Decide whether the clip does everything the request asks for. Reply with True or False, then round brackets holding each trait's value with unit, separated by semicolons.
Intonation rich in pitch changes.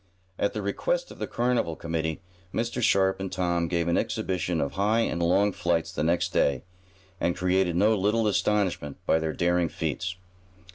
False (3.3 semitones)